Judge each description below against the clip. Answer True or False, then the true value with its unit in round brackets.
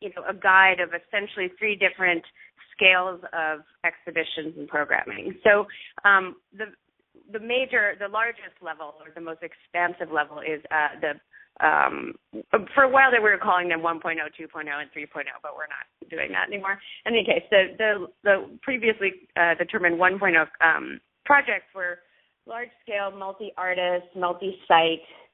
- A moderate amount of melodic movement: True (3.6 semitones)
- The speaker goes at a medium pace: True (155 wpm)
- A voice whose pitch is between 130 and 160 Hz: False (185 Hz)